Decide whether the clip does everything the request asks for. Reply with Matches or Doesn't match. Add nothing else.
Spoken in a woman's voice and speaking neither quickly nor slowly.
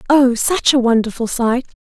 Matches